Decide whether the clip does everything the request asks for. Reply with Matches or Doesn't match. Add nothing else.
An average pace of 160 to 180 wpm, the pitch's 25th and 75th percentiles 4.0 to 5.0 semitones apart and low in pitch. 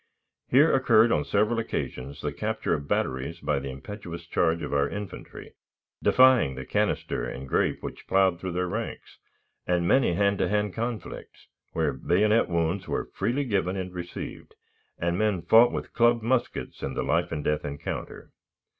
Doesn't match